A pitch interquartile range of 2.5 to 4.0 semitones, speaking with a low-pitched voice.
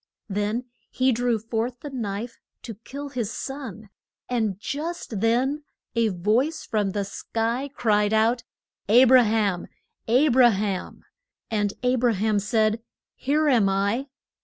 No: average, 3.4 semitones; high, 230 Hz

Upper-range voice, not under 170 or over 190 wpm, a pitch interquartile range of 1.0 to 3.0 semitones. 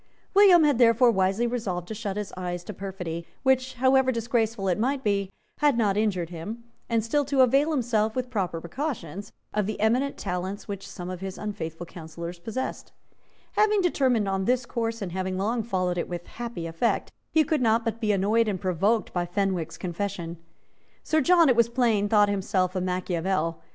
No: high, 210 Hz; average, 185 wpm; average, 4.7 semitones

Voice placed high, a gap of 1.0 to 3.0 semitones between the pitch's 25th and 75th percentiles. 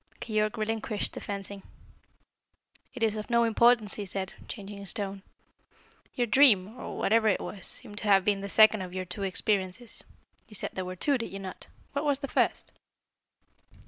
Yes: high, 210 Hz; average, 2.7 semitones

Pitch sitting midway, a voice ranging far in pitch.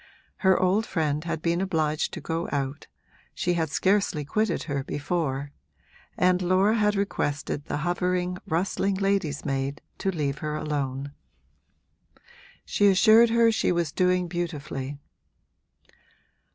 No: medium, 170 Hz; average, 4.5 semitones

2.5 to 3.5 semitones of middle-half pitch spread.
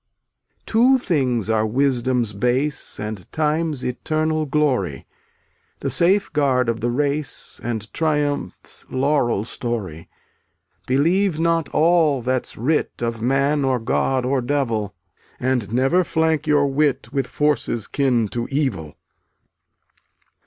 No: average, 4.2 semitones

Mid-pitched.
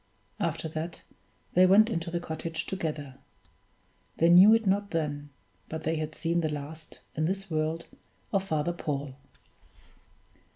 Yes: medium, 165 Hz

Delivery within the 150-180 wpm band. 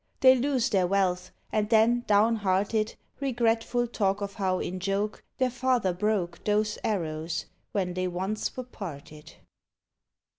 No: slow, 135 wpm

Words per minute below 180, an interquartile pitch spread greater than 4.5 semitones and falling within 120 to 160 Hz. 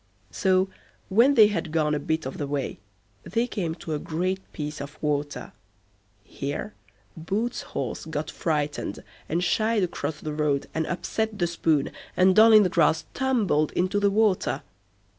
No: average, 160 wpm; average, 5.3 semitones; medium, 170 Hz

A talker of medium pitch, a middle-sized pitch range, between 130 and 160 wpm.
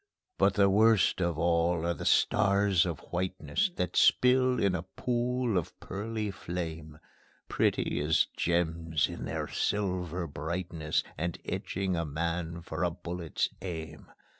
No: very low, 90 Hz; average, 3.1 semitones; average, 140 wpm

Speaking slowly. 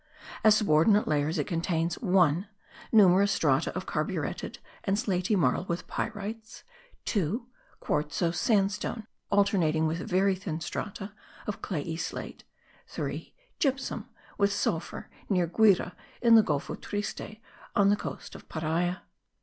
Yes: slow, 125 wpm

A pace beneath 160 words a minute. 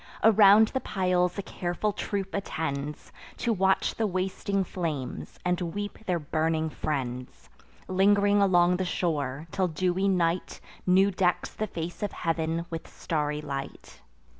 Yes: average, 140 wpm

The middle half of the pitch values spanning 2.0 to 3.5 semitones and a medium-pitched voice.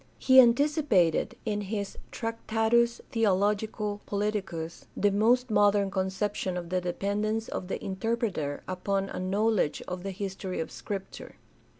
No: average, 2.9 semitones; high, 205 Hz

